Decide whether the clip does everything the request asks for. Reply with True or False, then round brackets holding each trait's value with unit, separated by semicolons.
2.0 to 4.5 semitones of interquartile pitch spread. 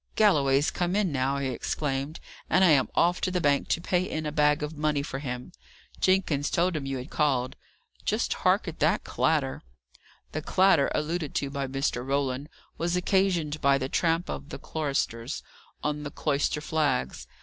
True (3.6 semitones)